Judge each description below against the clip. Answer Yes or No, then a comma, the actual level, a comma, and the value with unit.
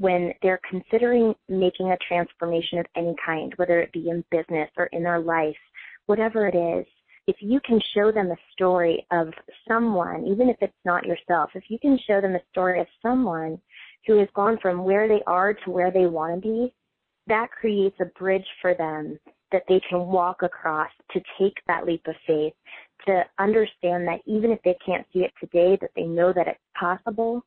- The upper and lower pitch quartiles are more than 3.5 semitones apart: No, average, 3.2 semitones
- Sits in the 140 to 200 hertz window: Yes, medium, 185 Hz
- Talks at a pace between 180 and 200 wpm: Yes, average, 195 wpm